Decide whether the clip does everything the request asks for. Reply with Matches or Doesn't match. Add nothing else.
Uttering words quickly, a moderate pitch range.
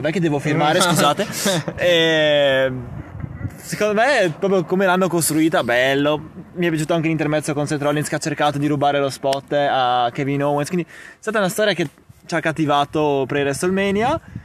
Matches